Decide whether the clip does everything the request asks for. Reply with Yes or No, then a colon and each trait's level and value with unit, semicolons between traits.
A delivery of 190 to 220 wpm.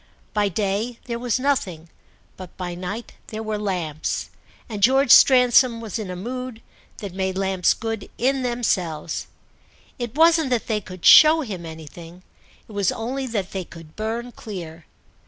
No: average, 155 wpm